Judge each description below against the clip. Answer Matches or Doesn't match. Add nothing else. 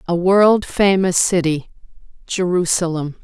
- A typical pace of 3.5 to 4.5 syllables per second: Matches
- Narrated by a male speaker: Doesn't match